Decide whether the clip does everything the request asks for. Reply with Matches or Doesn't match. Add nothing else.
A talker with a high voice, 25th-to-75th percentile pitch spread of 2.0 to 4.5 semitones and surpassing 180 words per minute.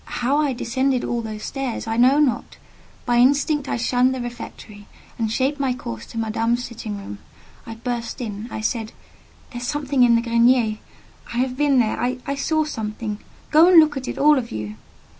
Matches